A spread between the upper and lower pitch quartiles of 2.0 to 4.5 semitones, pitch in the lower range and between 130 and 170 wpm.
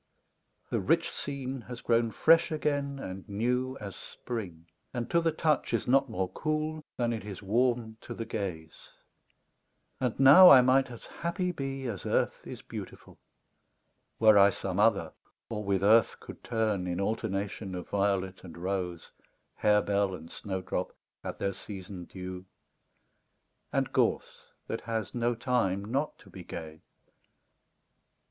No: average, 5.1 semitones; low, 110 Hz; average, 145 wpm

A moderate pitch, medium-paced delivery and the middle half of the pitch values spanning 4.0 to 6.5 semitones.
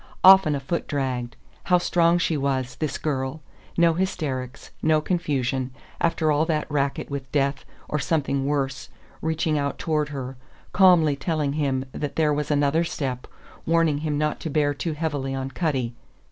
No: medium, 145 Hz; average, 160 wpm; average, 2.9 semitones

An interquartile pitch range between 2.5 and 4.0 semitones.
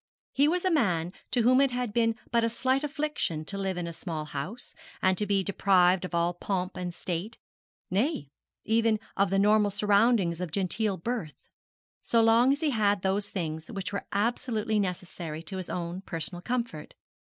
No: average, 4.5 semitones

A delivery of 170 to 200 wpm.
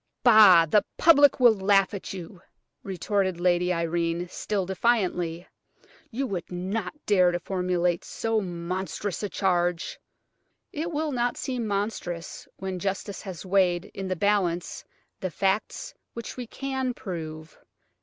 No: slow, 135 wpm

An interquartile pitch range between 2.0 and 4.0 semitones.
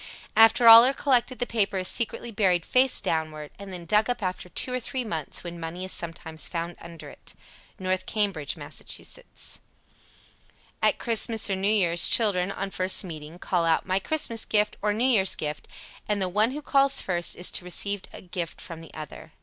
No: average, 4.7 semitones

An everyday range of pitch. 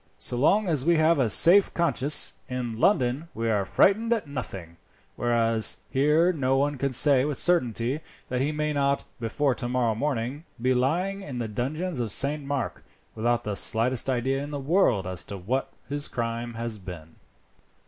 Yes: average, 4.4 semitones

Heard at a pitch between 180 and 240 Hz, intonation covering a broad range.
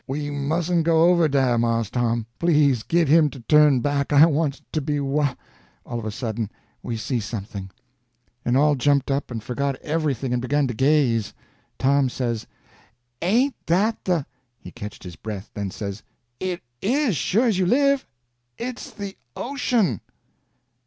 No: medium, 140 Hz; wide, 6.0 semitones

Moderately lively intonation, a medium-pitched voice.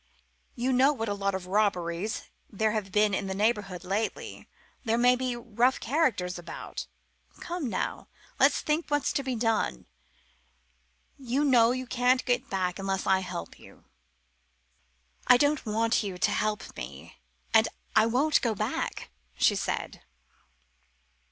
No: average, 4.4 semitones; high, 225 Hz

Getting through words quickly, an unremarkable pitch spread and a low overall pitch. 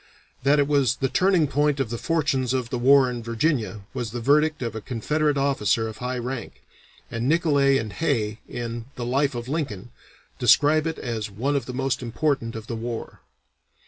No: average, 190 wpm; average, 3.8 semitones; low, 130 Hz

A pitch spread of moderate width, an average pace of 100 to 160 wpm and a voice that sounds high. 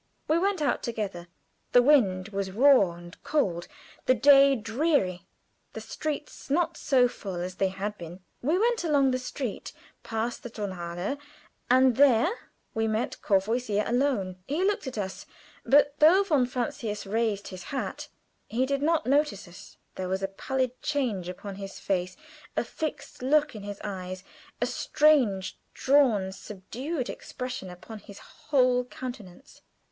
No: wide, 6.3 semitones; average, 150 wpm; high, 235 Hz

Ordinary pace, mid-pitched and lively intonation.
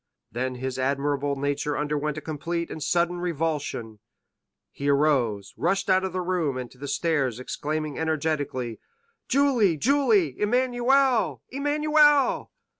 No: slow, 120 wpm; medium, 155 Hz; wide, 6.0 semitones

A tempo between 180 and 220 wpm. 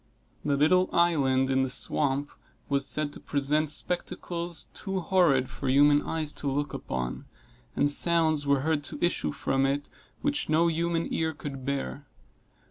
No: average, 155 wpm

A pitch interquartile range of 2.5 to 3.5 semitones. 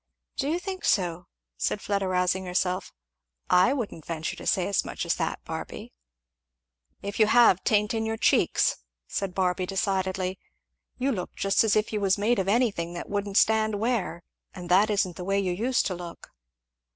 Yes: average, 3.1 semitones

